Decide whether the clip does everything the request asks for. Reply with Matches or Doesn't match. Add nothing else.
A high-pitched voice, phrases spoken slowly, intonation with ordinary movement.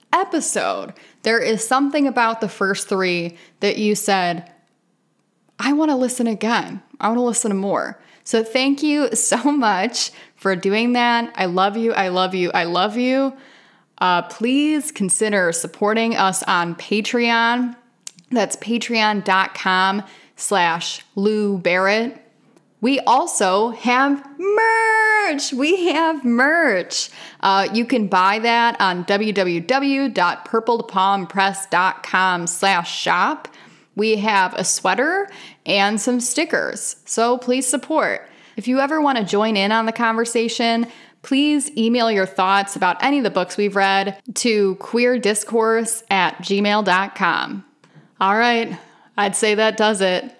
Matches